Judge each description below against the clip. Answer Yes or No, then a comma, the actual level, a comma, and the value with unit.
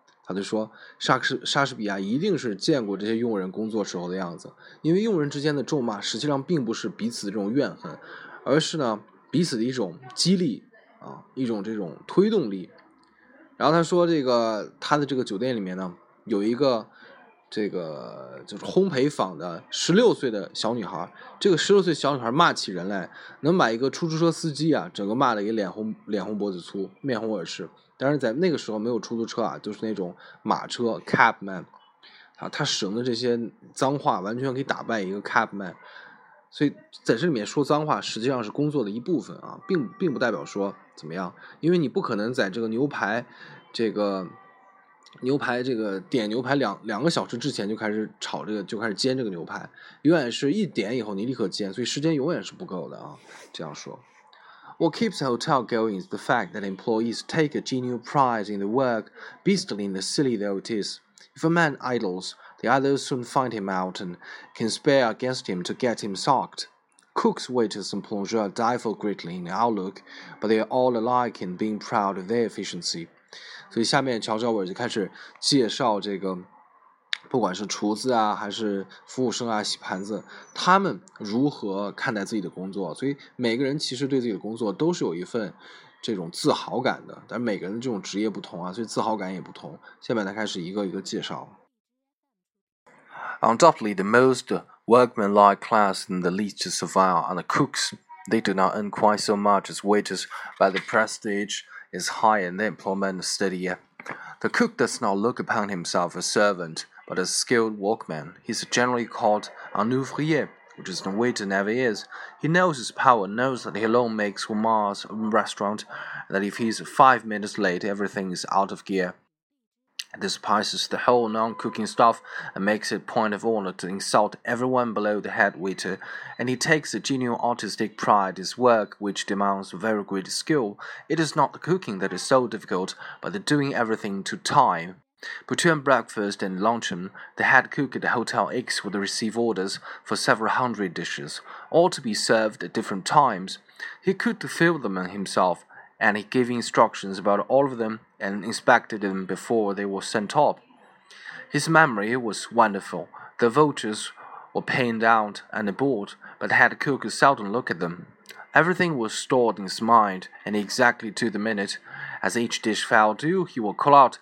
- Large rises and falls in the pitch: No, average, 5.0 semitones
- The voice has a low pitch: Yes, low, 115 Hz